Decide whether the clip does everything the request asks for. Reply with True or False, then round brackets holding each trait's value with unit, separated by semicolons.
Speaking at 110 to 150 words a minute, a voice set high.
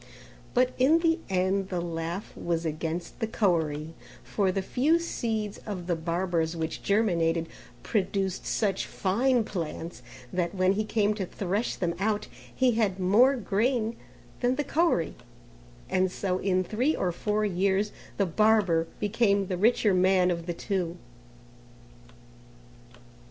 True (140 wpm; 195 Hz)